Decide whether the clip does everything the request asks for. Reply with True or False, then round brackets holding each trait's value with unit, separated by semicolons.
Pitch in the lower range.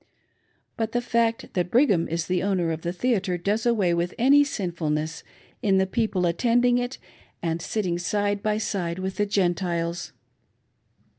False (190 Hz)